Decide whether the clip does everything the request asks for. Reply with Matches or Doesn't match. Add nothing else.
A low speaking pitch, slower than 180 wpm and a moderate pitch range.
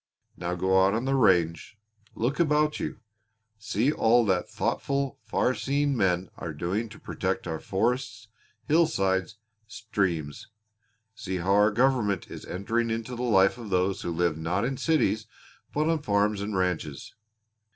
Matches